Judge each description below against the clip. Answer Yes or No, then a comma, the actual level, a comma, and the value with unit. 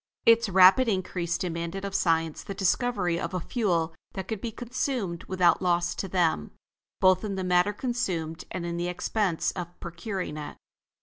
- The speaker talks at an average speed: Yes, average, 170 wpm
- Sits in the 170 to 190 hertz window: Yes, medium, 185 Hz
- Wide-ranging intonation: No, average, 2.7 semitones